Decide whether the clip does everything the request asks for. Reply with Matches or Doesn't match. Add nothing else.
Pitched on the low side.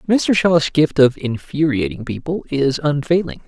Doesn't match